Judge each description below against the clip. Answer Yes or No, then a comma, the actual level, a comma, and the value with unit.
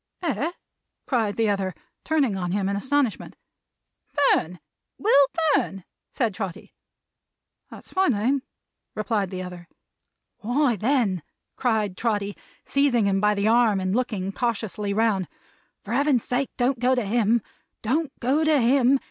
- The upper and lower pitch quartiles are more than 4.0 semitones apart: Yes, average, 4.8 semitones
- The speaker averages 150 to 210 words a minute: No, average, 140 wpm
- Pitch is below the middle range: No, high, 225 Hz